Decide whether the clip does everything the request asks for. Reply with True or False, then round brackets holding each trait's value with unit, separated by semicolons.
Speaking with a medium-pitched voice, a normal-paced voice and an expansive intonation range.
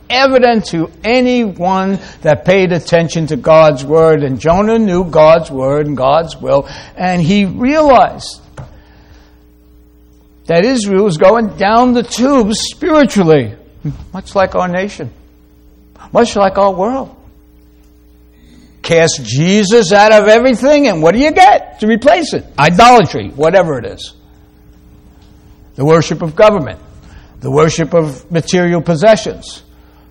False (165 Hz; 125 wpm; 8.5 semitones)